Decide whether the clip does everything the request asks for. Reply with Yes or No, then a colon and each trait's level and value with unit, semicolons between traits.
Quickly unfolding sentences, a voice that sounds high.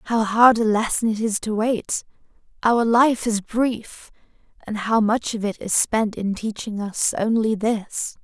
No: average, 175 wpm; high, 220 Hz